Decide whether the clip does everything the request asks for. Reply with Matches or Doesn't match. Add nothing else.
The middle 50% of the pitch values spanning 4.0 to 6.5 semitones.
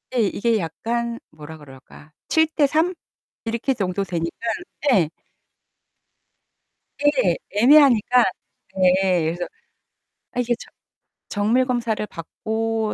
Matches